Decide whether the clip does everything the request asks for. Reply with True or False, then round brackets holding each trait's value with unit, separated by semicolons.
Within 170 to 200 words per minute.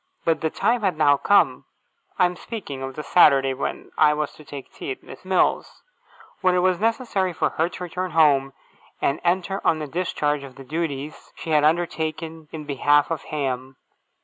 True (190 wpm)